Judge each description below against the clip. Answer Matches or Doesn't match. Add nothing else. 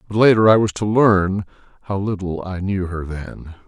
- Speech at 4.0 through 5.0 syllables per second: Matches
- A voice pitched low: Matches